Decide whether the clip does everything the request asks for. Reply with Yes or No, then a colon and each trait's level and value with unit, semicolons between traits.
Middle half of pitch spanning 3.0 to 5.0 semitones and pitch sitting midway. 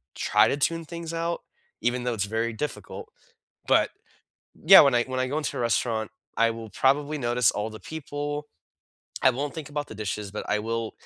No: average, 4.7 semitones; low, 125 Hz